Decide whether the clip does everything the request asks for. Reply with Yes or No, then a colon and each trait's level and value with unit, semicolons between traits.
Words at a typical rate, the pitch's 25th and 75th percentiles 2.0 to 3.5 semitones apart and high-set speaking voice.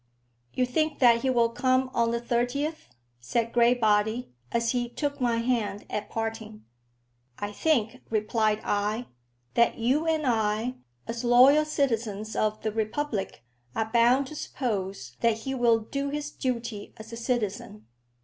Yes: average, 150 wpm; average, 2.9 semitones; high, 235 Hz